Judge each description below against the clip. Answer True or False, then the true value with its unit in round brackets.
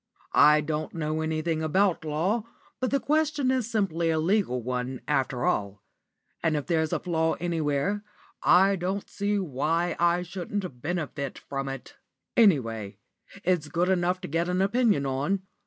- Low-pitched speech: False (165 Hz)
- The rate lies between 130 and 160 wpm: True (155 wpm)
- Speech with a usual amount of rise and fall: True (4.7 semitones)